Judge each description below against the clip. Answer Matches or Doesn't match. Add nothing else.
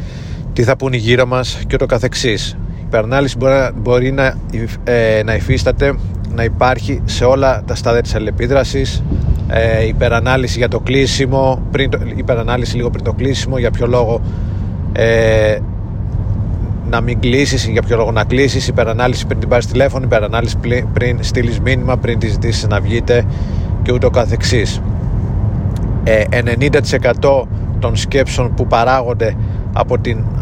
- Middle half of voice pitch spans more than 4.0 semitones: Doesn't match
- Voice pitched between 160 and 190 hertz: Doesn't match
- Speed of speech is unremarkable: Matches